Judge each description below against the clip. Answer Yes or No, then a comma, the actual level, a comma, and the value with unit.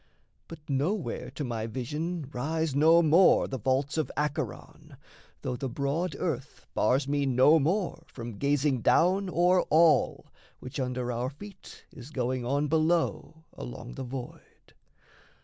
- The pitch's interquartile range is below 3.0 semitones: No, average, 4.1 semitones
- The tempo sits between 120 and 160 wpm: Yes, average, 140 wpm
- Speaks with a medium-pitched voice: Yes, medium, 145 Hz